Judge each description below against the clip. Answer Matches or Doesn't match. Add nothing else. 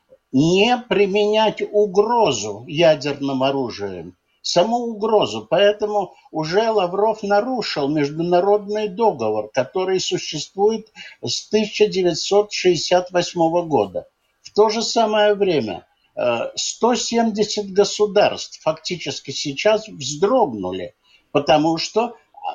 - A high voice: Matches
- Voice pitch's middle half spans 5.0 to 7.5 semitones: Matches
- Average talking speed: Doesn't match